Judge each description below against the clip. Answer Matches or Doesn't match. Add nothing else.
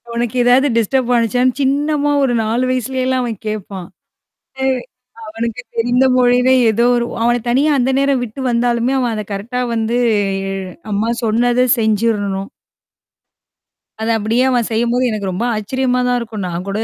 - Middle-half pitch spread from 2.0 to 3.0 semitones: Matches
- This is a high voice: Matches